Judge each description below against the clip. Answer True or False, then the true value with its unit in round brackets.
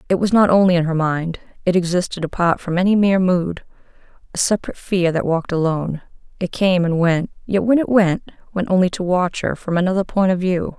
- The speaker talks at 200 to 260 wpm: True (205 wpm)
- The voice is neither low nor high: True (180 Hz)